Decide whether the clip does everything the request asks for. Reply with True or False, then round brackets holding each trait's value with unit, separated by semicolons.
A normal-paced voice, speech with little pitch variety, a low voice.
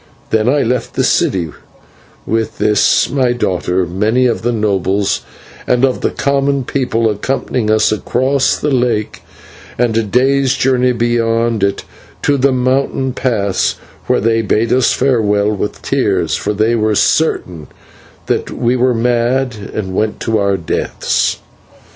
False (145 wpm; 3.3 semitones; 115 Hz)